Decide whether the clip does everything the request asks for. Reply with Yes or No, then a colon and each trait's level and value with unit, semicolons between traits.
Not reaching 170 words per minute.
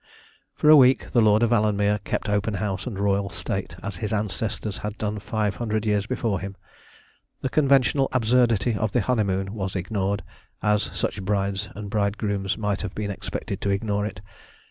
No: average, 175 wpm